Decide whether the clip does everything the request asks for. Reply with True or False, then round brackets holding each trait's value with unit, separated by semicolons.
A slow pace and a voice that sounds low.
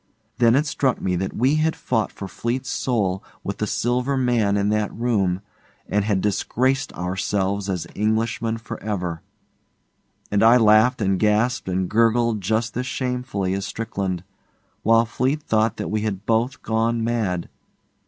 False (155 wpm; 110 Hz)